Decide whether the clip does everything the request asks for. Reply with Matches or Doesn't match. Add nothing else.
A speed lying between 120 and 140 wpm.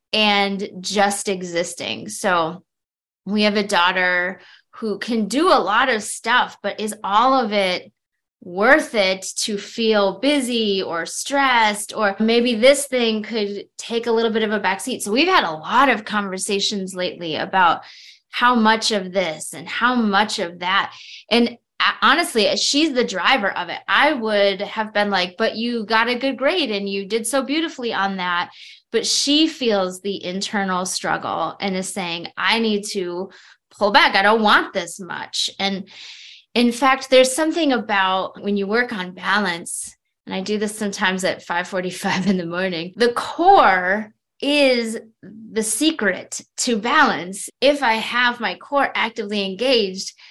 Doesn't match